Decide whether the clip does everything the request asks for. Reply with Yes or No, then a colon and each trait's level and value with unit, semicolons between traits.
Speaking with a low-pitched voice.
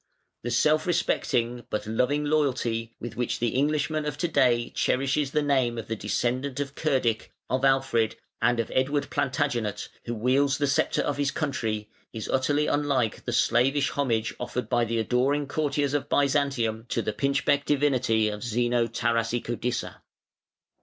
Yes: low, 130 Hz